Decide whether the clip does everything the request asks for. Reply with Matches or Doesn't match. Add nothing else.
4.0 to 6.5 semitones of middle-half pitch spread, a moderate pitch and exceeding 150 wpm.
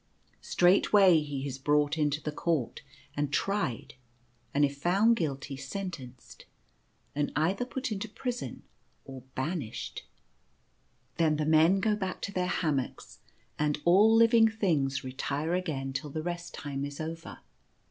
Doesn't match